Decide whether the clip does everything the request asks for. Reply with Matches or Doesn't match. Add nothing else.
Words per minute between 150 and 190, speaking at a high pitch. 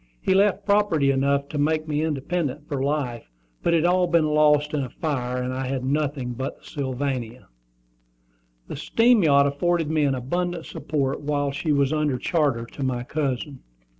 Doesn't match